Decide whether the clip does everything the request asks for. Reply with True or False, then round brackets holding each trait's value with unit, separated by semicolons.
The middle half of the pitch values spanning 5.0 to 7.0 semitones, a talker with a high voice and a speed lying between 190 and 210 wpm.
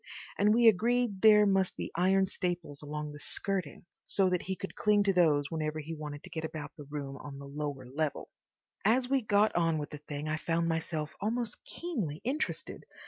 False (5.4 semitones; 170 Hz; 195 wpm)